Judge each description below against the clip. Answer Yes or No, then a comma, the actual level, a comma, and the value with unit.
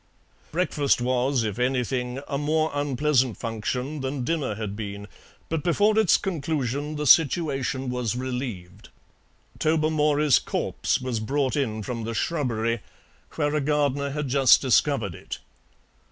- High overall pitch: No, low, 135 Hz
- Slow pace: Yes, slow, 130 wpm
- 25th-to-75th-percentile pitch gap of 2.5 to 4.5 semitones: Yes, average, 3.5 semitones